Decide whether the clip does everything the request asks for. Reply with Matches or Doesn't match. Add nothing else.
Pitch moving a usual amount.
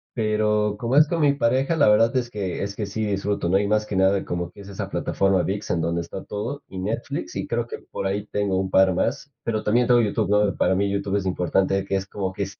Doesn't match